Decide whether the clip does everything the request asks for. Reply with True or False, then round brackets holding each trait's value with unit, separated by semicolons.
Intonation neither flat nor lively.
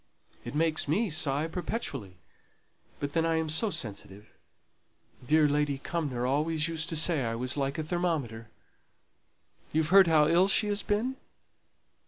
True (3.5 semitones)